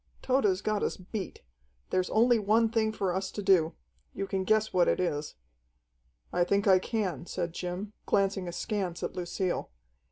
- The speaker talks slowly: No, average, 165 wpm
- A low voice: No, high, 190 Hz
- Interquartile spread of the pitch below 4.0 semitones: Yes, average, 3.1 semitones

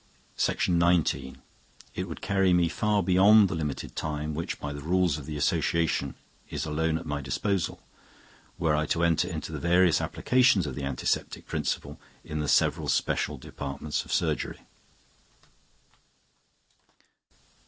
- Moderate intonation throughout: Yes, average, 3.4 semitones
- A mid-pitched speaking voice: No, very low, 80 Hz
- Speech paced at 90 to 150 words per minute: Yes, slow, 135 wpm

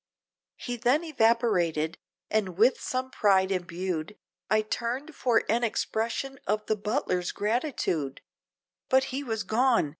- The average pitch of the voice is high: Yes, high, 220 Hz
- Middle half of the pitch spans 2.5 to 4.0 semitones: No, average, 4.9 semitones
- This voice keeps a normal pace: No, slow, 125 wpm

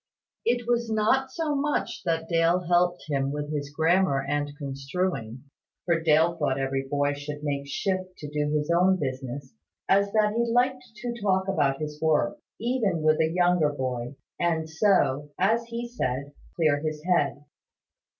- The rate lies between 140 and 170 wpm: Yes, average, 160 wpm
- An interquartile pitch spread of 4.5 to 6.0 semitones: Yes, average, 5.2 semitones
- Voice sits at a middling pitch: Yes, medium, 160 Hz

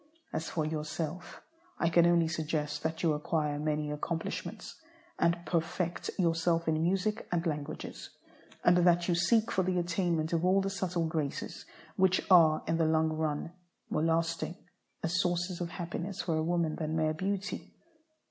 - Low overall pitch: No, medium, 165 Hz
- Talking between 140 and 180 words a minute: Yes, average, 160 wpm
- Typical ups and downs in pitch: No, narrow, 2.0 semitones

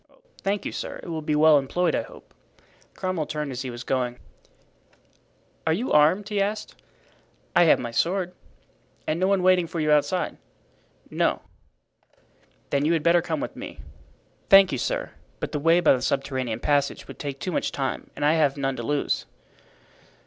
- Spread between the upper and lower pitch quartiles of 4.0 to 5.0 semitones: Yes, average, 4.4 semitones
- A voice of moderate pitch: Yes, medium, 155 Hz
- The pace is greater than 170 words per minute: Yes, average, 180 wpm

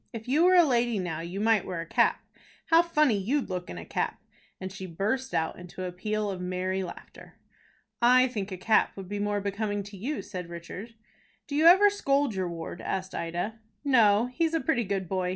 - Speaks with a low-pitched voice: No, high, 205 Hz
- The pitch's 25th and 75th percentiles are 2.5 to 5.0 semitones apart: No, wide, 5.4 semitones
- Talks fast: Yes, fast, 210 wpm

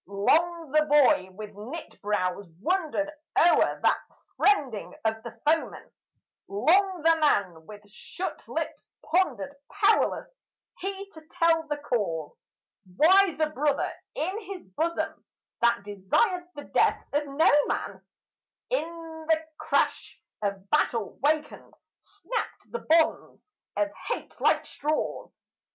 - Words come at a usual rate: No, slow, 120 wpm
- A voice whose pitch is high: Yes, very high, 305 Hz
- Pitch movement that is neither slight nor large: No, wide, 7.5 semitones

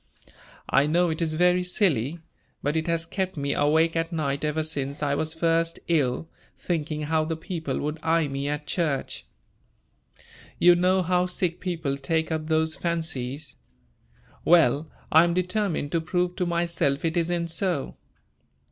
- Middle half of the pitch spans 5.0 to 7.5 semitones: No, narrow, 2.6 semitones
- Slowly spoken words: No, average, 155 wpm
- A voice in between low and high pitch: Yes, medium, 160 Hz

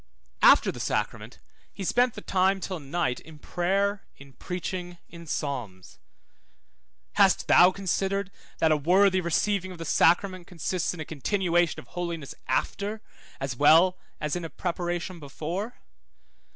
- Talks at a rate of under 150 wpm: Yes, average, 140 wpm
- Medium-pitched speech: Yes, medium, 175 Hz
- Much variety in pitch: No, average, 3.3 semitones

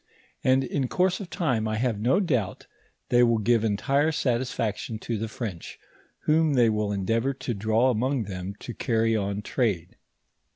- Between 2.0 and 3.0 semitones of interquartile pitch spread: No, average, 3.5 semitones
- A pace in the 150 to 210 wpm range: Yes, average, 170 wpm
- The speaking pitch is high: No, low, 115 Hz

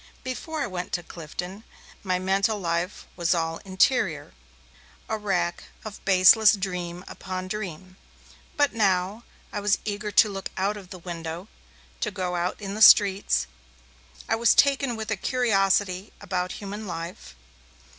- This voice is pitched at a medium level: No, high, 195 Hz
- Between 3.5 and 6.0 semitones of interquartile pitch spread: No, average, 2.8 semitones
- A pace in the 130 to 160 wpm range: Yes, average, 145 wpm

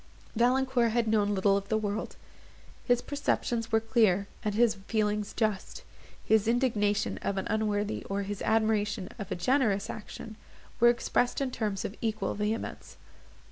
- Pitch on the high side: Yes, high, 215 Hz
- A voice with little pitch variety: Yes, narrow, 2.2 semitones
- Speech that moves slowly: No, average, 150 wpm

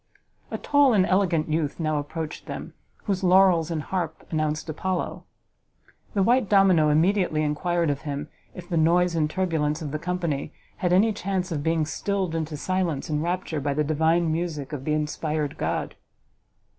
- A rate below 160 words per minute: No, average, 170 wpm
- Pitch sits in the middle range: Yes, medium, 165 Hz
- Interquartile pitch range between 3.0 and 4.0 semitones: Yes, average, 3.3 semitones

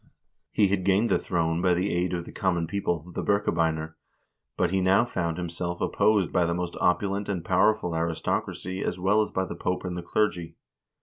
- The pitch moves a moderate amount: No, narrow, 2.3 semitones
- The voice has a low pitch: Yes, very low, 90 Hz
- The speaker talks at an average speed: Yes, average, 195 wpm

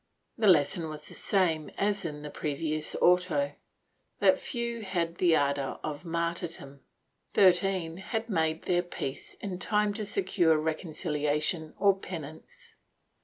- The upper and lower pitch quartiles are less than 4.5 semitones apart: Yes, average, 3.8 semitones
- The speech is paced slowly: Yes, slow, 130 wpm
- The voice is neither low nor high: Yes, medium, 170 Hz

